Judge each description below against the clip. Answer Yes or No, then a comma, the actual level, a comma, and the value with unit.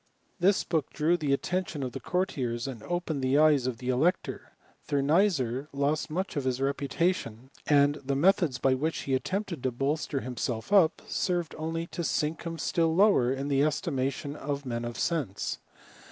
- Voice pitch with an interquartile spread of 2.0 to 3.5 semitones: No, average, 4.2 semitones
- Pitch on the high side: No, medium, 145 Hz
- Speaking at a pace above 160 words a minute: Yes, average, 180 wpm